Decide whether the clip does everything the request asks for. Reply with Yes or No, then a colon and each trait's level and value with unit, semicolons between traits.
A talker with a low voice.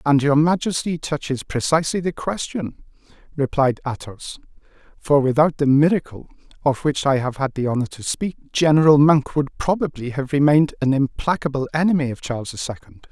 No: medium, 145 Hz